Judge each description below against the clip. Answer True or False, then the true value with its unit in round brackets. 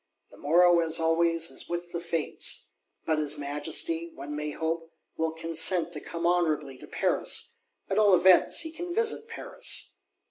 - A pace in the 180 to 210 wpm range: False (165 wpm)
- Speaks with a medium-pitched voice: True (165 Hz)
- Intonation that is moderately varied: False (2.2 semitones)